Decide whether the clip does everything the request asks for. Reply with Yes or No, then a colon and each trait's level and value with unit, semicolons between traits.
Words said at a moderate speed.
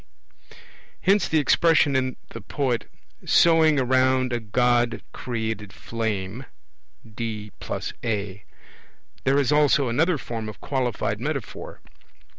No: slow, 110 wpm